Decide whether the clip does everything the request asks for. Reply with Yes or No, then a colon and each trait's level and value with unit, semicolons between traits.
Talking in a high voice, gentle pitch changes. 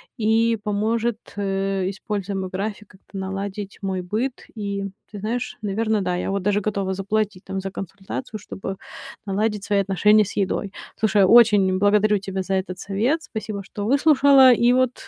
Yes: high, 205 Hz; narrow, 2.0 semitones